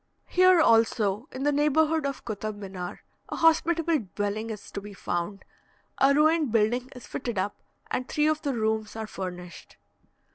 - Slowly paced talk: No, average, 160 wpm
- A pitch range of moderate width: No, wide, 6.5 semitones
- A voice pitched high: Yes, high, 230 Hz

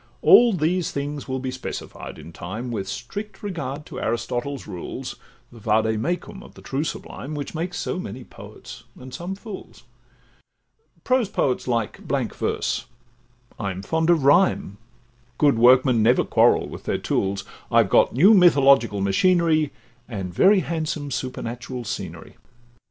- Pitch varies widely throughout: Yes, wide, 6.7 semitones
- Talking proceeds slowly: No, average, 145 wpm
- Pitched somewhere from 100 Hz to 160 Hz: Yes, low, 135 Hz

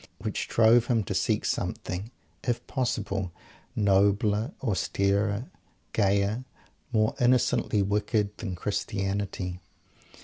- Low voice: Yes, low, 105 Hz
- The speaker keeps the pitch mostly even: Yes, narrow, 2.2 semitones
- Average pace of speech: No, slow, 95 wpm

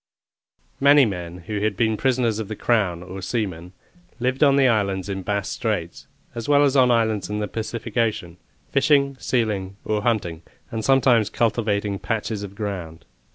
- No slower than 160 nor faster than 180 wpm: Yes, average, 165 wpm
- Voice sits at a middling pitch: No, low, 110 Hz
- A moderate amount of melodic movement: Yes, average, 3.5 semitones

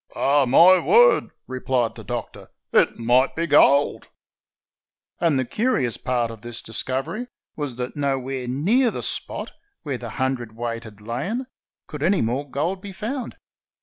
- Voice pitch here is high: No, low, 135 Hz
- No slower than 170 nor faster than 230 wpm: No, average, 150 wpm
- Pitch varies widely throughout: Yes, wide, 5.9 semitones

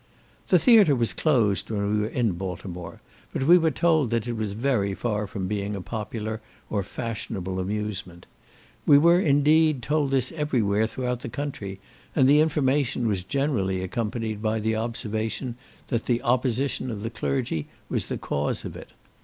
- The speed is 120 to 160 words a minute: No, average, 170 wpm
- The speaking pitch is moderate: No, low, 115 Hz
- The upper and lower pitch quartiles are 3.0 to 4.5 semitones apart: No, average, 5.1 semitones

